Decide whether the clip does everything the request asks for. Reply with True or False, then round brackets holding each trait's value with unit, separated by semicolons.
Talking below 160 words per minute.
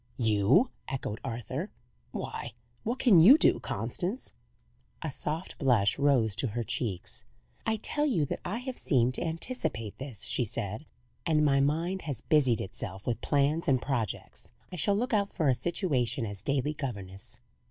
False (165 wpm)